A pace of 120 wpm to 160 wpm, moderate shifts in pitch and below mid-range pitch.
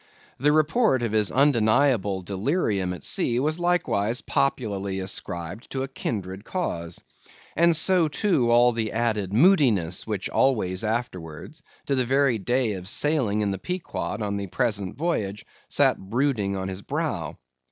No: average, 150 wpm; wide, 6.2 semitones; low, 115 Hz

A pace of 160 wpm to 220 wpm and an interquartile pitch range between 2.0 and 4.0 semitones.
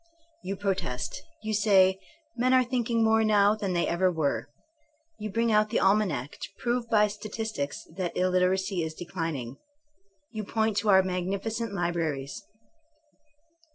No: average, 140 wpm; average, 3.7 semitones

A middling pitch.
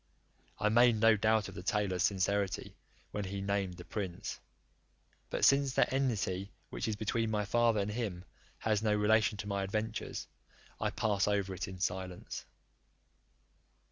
No: low, 105 Hz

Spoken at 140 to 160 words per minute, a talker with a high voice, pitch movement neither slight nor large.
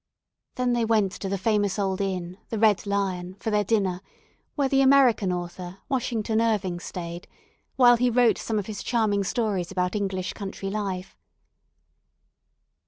Yes: average, 155 wpm; high, 205 Hz; average, 3.4 semitones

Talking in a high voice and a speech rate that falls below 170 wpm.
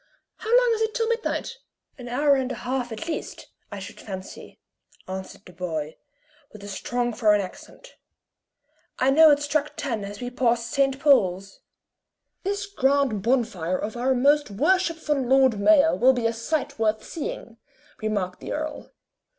Yes: very high, 255 Hz; average, 160 wpm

